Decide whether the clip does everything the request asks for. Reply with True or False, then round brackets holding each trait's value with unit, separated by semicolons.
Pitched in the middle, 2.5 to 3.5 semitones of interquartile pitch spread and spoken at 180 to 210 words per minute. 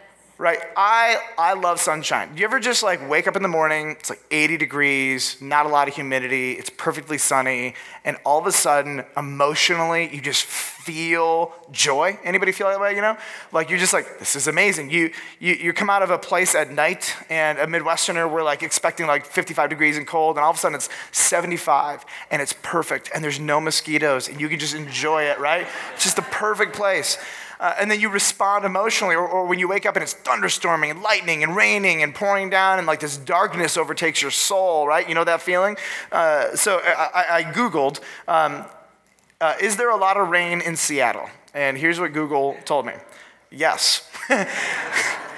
False (165 Hz; 4.1 semitones; 200 wpm)